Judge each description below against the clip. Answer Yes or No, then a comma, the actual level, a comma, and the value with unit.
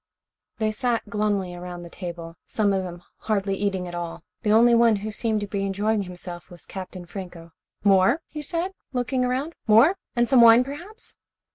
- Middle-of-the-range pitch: No, high, 210 Hz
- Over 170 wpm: Yes, average, 180 wpm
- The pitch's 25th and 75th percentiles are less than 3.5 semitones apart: No, average, 4.8 semitones